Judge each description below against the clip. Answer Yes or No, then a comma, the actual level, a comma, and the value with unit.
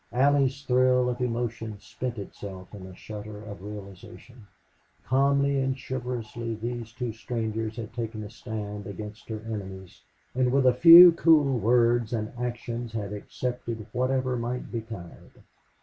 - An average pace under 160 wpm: Yes, average, 140 wpm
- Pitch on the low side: Yes, low, 115 Hz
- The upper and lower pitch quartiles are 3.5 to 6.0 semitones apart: No, average, 2.9 semitones